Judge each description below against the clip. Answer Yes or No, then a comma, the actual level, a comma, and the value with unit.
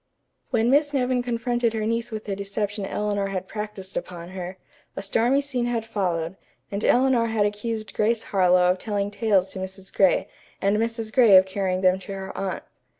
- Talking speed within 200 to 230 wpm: No, average, 185 wpm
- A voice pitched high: Yes, high, 205 Hz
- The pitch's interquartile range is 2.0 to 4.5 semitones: Yes, average, 3.3 semitones